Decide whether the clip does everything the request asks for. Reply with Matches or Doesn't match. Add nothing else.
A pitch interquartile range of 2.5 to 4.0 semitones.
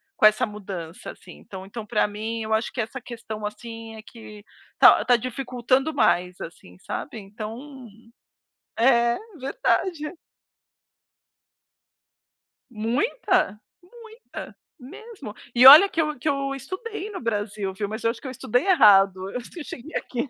Doesn't match